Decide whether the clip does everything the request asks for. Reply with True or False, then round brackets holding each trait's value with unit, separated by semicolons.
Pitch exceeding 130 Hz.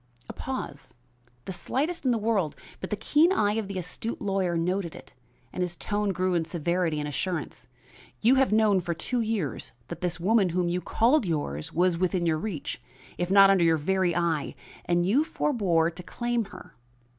True (185 Hz)